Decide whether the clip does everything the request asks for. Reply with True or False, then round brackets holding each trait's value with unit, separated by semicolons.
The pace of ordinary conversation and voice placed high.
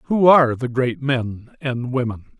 False (175 wpm; 130 Hz)